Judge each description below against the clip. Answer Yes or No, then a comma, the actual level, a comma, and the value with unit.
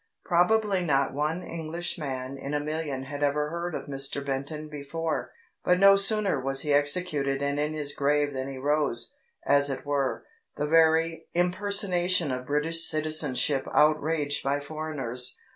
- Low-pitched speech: No, medium, 150 Hz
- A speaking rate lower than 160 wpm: Yes, average, 150 wpm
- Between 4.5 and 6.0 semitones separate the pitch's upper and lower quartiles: No, average, 2.9 semitones